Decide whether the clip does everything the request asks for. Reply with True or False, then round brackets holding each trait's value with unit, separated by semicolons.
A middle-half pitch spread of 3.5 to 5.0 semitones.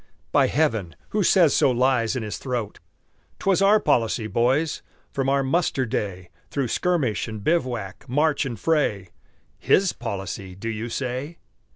False (5.6 semitones)